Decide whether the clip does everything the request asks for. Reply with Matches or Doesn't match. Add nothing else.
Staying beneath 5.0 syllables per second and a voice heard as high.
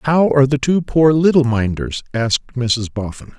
Doesn't match